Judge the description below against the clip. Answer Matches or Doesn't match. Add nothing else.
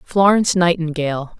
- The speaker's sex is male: Doesn't match